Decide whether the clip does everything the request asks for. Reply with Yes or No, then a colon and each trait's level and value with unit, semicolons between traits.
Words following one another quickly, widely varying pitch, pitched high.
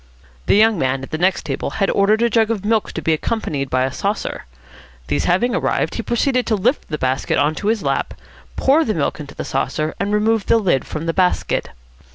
Yes: fast, 220 wpm; wide, 6.8 semitones; high, 195 Hz